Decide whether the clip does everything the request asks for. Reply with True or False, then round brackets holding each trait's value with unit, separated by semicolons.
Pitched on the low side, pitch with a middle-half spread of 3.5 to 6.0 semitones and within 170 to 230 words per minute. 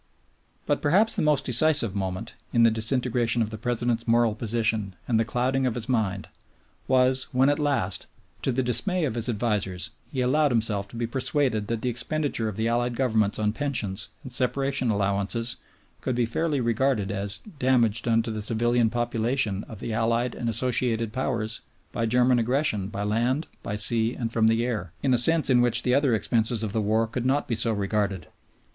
False (115 Hz; 2.7 semitones; 190 wpm)